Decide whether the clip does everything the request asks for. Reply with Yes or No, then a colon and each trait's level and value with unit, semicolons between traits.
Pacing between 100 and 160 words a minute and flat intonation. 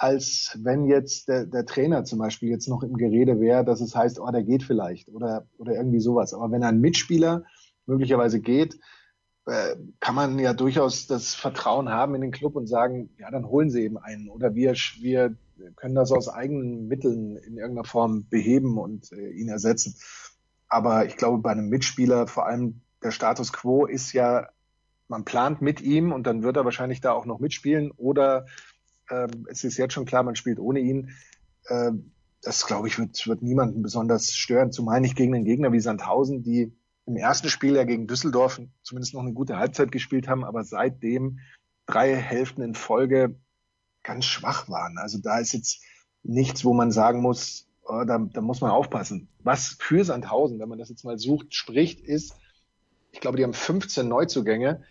No: average, 185 wpm; narrow, 2.2 semitones